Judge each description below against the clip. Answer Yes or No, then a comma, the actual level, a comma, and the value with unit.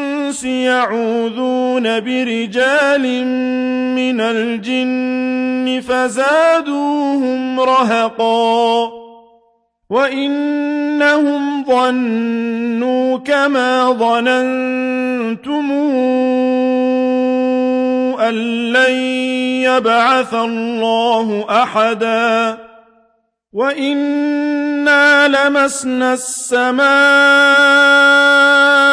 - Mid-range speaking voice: No, very high, 255 Hz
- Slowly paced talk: Yes, slow, 35 wpm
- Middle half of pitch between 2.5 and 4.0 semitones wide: Yes, average, 3.2 semitones